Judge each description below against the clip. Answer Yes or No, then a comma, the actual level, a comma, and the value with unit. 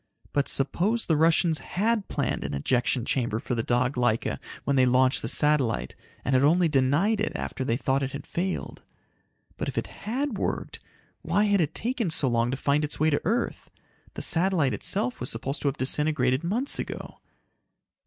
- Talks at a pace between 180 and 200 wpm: Yes, average, 185 wpm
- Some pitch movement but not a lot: No, wide, 5.8 semitones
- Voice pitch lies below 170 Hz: Yes, medium, 140 Hz